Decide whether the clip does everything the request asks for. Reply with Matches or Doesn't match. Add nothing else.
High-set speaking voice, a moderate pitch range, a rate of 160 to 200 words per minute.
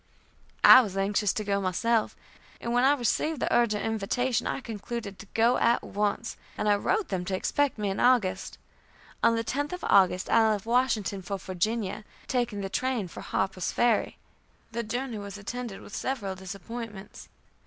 Matches